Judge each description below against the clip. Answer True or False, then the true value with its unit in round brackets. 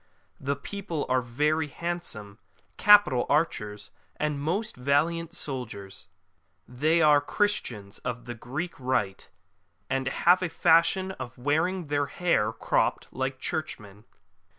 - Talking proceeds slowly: True (120 wpm)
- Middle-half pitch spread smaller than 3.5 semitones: False (5.5 semitones)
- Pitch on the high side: False (145 Hz)